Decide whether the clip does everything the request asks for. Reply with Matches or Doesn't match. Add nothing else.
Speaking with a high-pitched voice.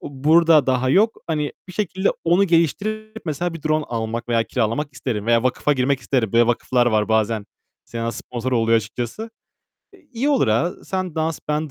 Doesn't match